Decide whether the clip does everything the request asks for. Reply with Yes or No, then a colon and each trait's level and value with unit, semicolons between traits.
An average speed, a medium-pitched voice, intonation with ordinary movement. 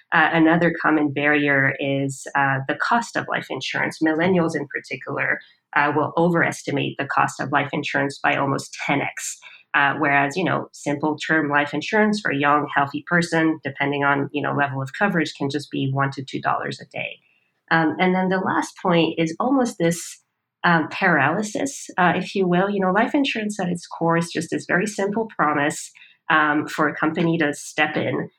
Yes: average, 185 wpm; medium, 155 Hz; average, 3.7 semitones